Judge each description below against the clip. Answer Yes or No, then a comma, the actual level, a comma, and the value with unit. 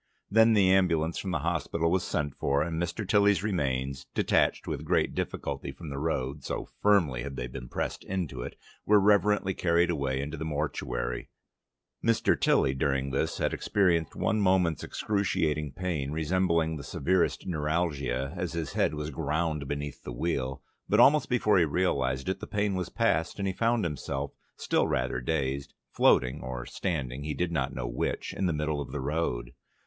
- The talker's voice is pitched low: Yes, very low, 80 Hz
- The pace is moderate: Yes, average, 175 wpm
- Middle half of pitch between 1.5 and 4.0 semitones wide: No, average, 5.0 semitones